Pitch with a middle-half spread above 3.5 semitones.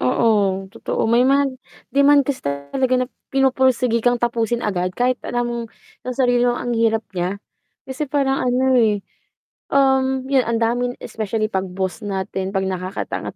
Yes: average, 4.5 semitones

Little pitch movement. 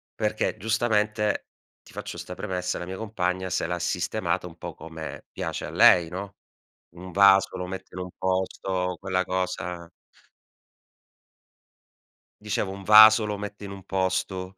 Yes: narrow, 1.9 semitones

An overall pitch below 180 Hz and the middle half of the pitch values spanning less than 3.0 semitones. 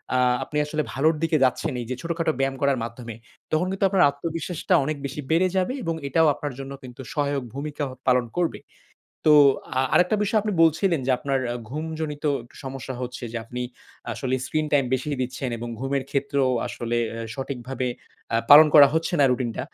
No: medium, 140 Hz; average, 3.6 semitones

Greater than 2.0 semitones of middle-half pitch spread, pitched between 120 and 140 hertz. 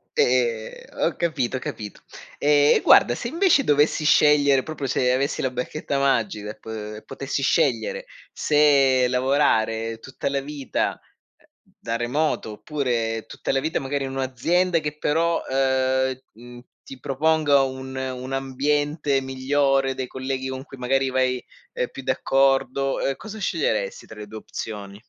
Yes: narrow, 2.5 semitones; low, 135 Hz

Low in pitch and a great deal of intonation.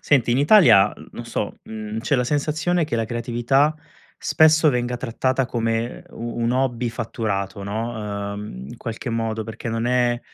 No: low, 120 Hz; average, 2.7 semitones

